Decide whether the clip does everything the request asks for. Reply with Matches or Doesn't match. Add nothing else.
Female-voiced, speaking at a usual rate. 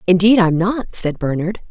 Matches